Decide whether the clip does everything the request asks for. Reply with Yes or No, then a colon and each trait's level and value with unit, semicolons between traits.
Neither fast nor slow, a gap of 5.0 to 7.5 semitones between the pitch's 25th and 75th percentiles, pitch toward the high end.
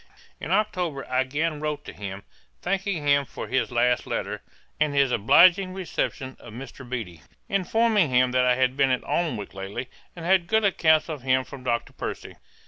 No: average, 180 wpm; wide, 5.6 semitones; medium, 140 Hz